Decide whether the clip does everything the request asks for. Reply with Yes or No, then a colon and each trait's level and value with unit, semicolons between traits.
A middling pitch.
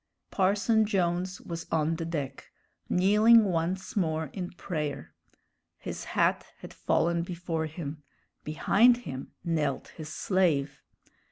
Yes: medium, 170 Hz